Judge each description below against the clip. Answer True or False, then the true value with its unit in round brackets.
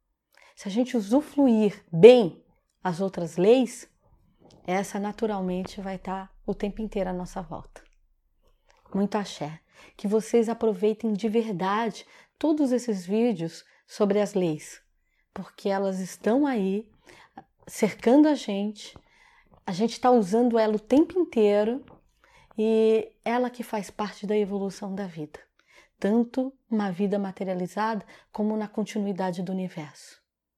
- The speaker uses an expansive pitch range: False (3.0 semitones)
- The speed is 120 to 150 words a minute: True (125 wpm)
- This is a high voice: True (210 Hz)